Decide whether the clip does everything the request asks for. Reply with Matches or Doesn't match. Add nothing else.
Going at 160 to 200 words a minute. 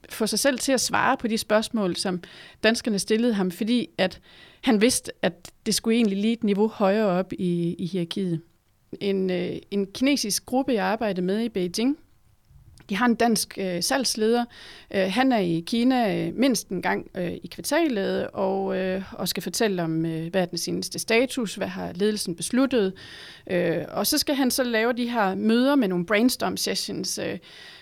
Matches